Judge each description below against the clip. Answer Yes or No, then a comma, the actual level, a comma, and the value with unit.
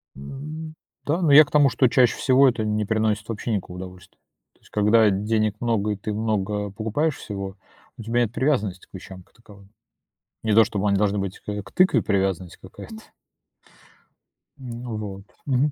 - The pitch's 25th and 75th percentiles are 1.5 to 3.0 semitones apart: No, average, 3.8 semitones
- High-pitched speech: No, low, 110 Hz